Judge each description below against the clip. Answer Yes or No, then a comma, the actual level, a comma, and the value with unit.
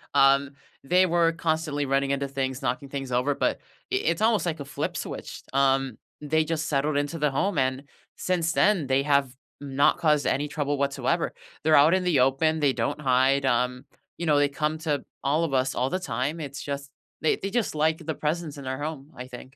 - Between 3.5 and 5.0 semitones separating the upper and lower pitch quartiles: No, average, 2.7 semitones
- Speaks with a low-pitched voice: No, medium, 145 Hz